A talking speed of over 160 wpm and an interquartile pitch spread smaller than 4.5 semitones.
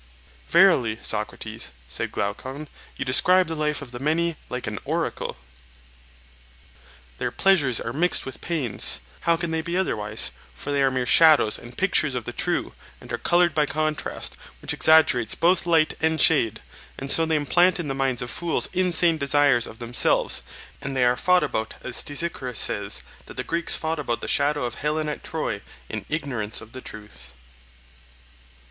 No: average, 170 wpm; average, 5.1 semitones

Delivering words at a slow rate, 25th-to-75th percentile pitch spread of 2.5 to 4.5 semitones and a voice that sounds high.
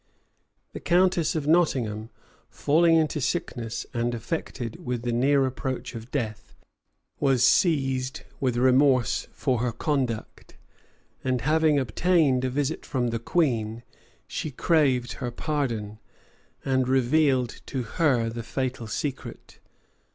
No: slow, 120 wpm; average, 3.6 semitones; low, 130 Hz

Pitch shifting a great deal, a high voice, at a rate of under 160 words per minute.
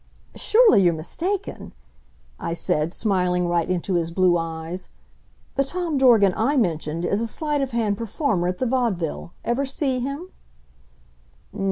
Yes: wide, 7.6 semitones; high, 205 Hz; average, 145 wpm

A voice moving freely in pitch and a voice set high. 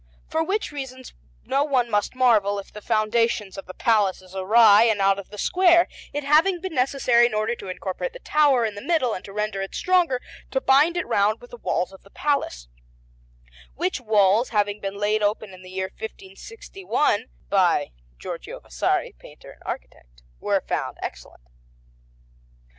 Yes: wide, 5.9 semitones; high, 220 Hz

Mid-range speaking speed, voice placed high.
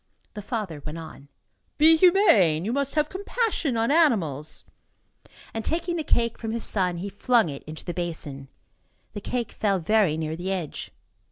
Yes: average, 170 wpm; high, 210 Hz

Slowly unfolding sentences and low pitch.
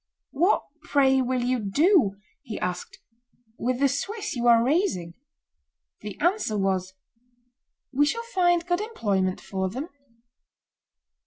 No: slow, 120 wpm; very high, 255 Hz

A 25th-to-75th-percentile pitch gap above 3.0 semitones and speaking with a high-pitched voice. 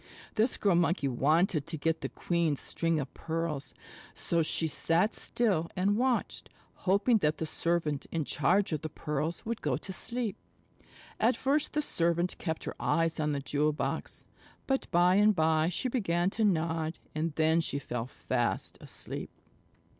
No: average, 3.9 semitones; medium, 165 Hz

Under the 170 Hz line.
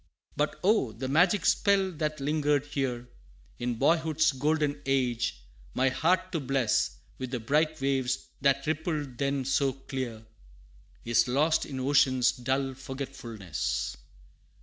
Yes: low, 135 Hz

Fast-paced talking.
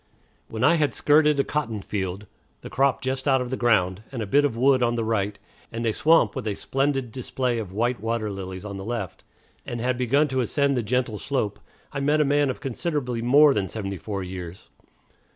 Yes: fast, 215 wpm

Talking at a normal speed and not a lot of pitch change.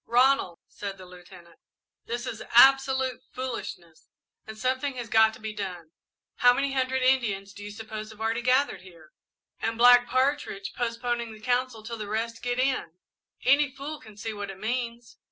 No: average, 170 wpm; average, 3.7 semitones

